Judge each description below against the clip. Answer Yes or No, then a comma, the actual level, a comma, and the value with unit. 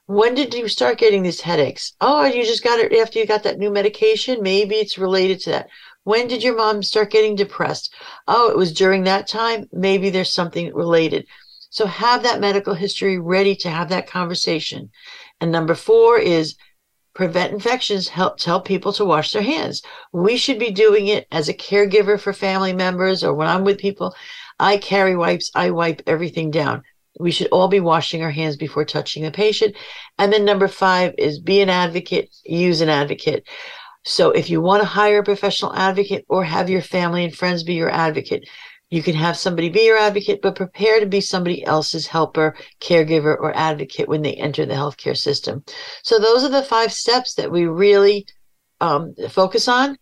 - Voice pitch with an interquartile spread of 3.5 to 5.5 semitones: Yes, average, 4.3 semitones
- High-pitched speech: Yes, high, 200 Hz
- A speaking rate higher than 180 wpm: Yes, average, 195 wpm